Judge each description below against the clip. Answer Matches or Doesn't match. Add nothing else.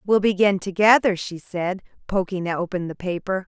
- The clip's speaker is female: Matches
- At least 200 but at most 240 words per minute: Doesn't match